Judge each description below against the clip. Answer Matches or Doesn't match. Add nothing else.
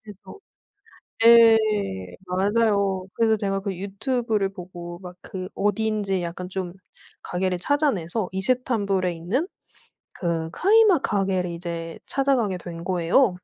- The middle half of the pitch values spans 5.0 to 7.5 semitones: Doesn't match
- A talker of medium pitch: Doesn't match